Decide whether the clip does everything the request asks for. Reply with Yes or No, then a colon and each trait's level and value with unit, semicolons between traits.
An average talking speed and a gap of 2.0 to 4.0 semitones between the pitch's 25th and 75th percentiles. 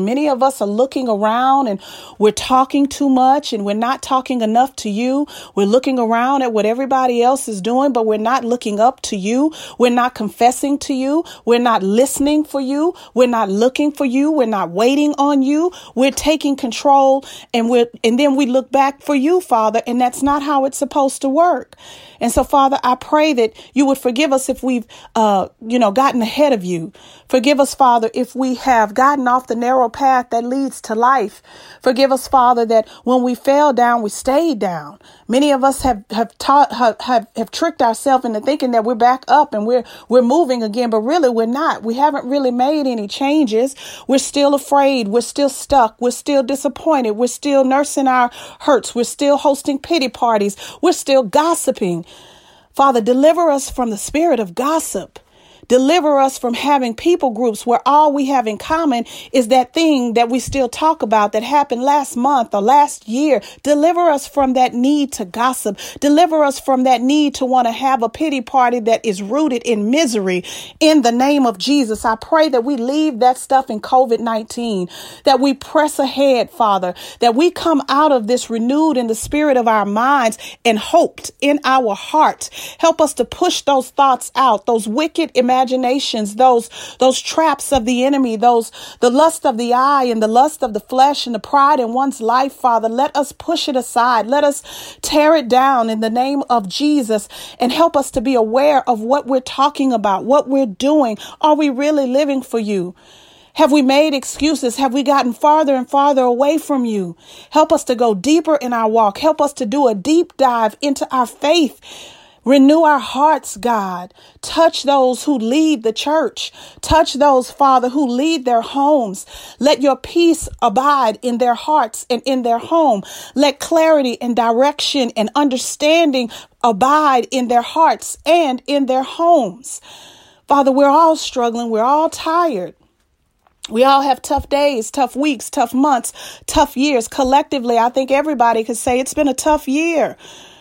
Yes: average, 190 wpm; average, 3.3 semitones